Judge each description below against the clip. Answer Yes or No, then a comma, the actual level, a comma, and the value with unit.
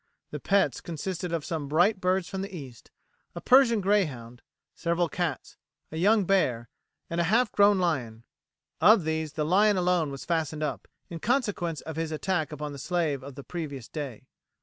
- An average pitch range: Yes, average, 4.5 semitones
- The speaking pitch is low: No, medium, 165 Hz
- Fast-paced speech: No, average, 175 wpm